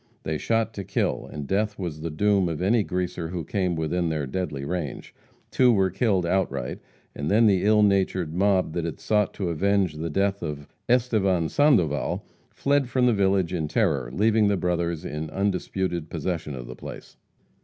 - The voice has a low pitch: Yes, very low, 90 Hz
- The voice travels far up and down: No, average, 4.0 semitones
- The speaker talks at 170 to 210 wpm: Yes, average, 180 wpm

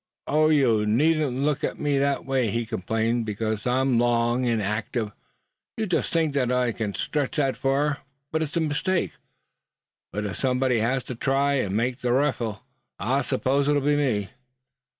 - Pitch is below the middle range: Yes, low, 130 Hz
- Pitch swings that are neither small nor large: Yes, average, 3.8 semitones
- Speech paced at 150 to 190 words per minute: Yes, average, 170 wpm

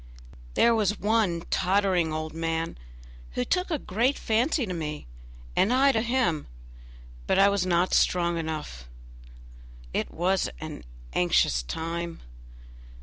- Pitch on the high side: No, medium, 180 Hz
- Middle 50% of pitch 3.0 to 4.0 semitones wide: No, average, 5.3 semitones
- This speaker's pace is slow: Yes, slow, 130 wpm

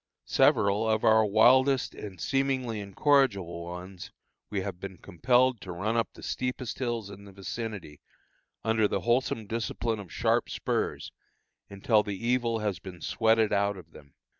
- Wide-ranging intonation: No, average, 3.2 semitones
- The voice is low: Yes, low, 110 Hz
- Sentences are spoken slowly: No, average, 155 wpm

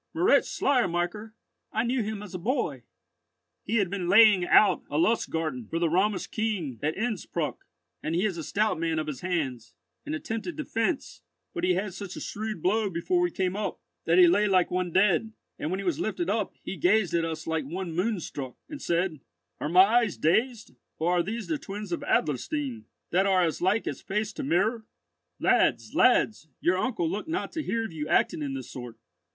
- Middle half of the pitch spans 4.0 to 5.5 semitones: Yes, average, 4.8 semitones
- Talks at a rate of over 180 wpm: Yes, average, 200 wpm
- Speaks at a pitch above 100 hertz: Yes, high, 190 Hz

